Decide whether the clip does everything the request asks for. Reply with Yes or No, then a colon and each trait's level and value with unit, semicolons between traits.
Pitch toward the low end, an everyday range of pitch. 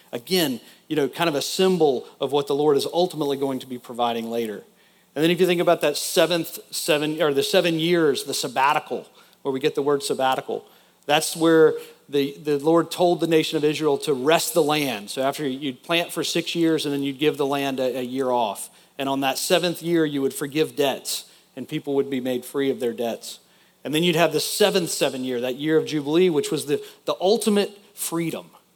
No: medium, 150 Hz; average, 3.7 semitones